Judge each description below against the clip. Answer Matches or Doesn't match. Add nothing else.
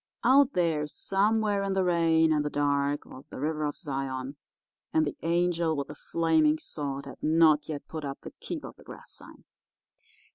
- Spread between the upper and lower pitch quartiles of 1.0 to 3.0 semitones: Matches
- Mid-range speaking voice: Matches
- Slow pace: Doesn't match